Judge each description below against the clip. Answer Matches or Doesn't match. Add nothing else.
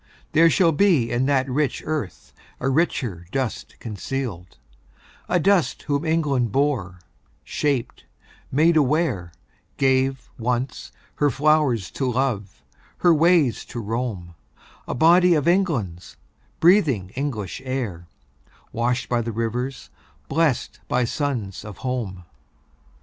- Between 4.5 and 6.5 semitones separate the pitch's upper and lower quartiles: Matches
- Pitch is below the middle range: Matches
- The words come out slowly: Matches